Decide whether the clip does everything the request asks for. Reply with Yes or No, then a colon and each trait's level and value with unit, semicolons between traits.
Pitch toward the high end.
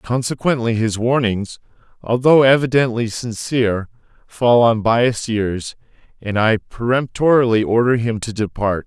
No: low, 115 Hz